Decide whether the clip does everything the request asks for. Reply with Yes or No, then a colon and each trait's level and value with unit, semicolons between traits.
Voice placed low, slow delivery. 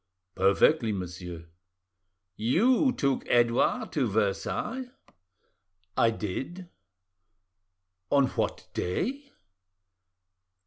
Yes: low, 120 Hz; slow, 70 wpm